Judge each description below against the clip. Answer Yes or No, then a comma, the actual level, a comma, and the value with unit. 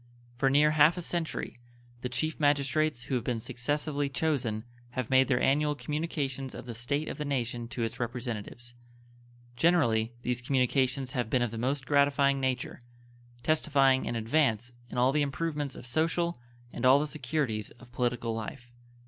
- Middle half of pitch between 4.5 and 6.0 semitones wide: No, average, 3.5 semitones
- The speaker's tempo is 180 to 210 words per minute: No, average, 165 wpm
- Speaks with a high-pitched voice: No, low, 130 Hz